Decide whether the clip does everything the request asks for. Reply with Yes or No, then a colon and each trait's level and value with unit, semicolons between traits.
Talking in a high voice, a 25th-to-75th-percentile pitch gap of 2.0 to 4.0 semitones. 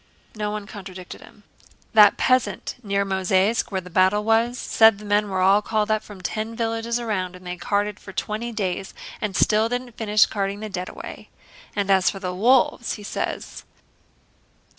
Yes: high, 210 Hz; narrow, 2.5 semitones